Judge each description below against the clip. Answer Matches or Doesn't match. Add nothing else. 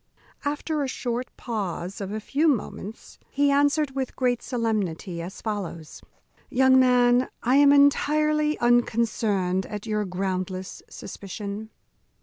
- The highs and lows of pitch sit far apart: Matches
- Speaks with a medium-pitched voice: Doesn't match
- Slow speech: Matches